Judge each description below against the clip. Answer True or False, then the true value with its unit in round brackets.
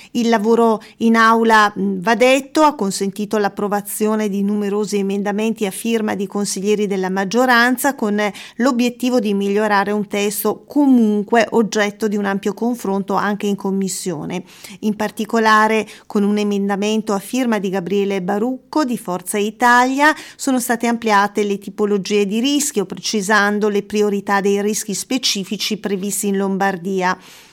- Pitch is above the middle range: True (210 Hz)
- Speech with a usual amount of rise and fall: False (2.3 semitones)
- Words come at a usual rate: True (135 wpm)